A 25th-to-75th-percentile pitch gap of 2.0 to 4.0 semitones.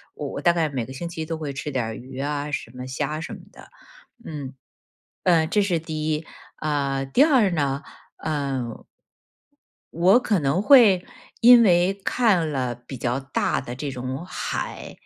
No: average, 4.6 semitones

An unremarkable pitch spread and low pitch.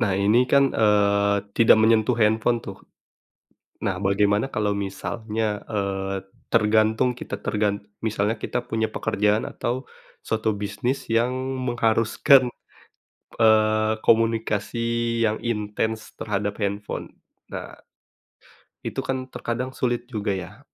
No: narrow, 2.0 semitones; low, 110 Hz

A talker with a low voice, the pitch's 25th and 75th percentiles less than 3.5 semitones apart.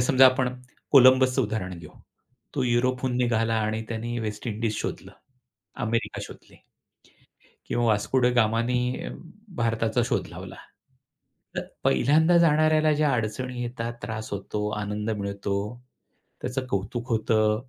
Yes: low, 120 Hz; average, 2.8 semitones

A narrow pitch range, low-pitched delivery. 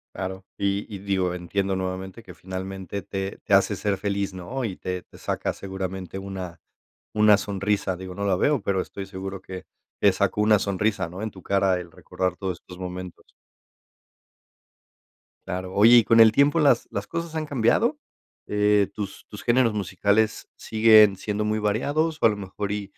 Yes: narrow, 2.2 semitones; low, 100 Hz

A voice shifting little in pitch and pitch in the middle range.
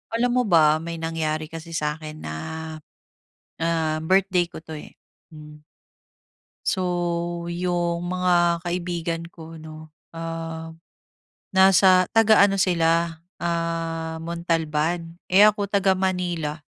Yes: narrow, 1.8 semitones; medium, 170 Hz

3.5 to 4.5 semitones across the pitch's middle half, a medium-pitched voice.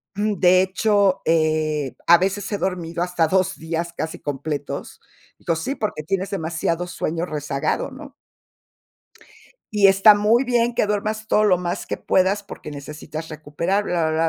Yes: average, 4.2 semitones; medium, 180 Hz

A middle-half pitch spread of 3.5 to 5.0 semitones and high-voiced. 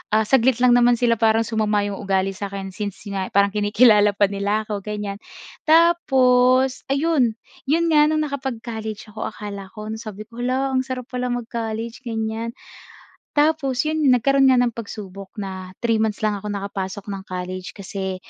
Yes: average, 3.9 semitones; high, 220 Hz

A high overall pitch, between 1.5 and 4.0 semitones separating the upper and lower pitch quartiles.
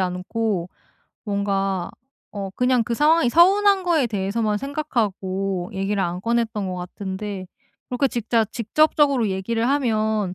No: high, 215 Hz; average, 4.4 semitones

